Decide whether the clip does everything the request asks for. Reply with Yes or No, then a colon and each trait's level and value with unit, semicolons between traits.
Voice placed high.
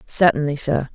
No: medium, 145 Hz